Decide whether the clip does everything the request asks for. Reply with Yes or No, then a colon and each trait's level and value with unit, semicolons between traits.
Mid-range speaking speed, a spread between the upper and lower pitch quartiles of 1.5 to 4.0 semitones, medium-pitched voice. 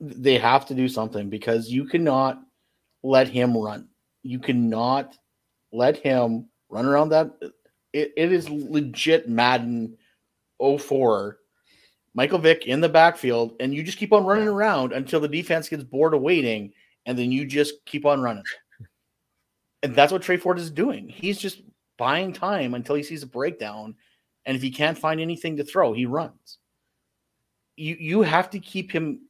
No: average, 170 wpm; average, 4.9 semitones; medium, 145 Hz